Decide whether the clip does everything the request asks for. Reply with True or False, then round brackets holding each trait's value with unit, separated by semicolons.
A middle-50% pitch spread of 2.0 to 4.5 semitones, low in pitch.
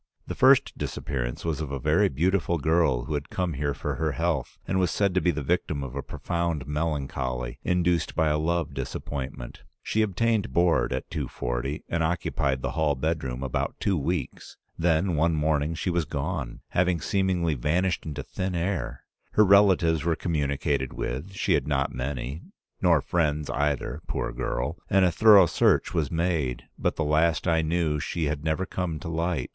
True (3.6 semitones; 80 Hz)